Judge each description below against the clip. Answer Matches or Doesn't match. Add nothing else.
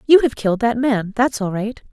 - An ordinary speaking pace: Doesn't match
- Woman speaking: Matches